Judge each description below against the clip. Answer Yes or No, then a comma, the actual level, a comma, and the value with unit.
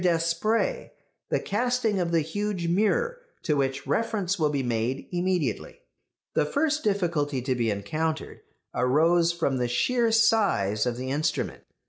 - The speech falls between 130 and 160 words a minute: Yes, average, 140 wpm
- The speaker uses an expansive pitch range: Yes, wide, 7.7 semitones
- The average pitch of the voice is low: No, medium, 170 Hz